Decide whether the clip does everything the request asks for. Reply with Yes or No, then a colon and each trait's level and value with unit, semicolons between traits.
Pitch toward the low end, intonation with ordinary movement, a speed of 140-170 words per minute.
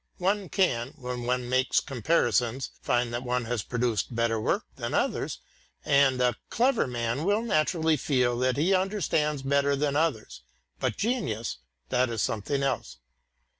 Yes: low, 130 Hz; average, 4.4 semitones; average, 150 wpm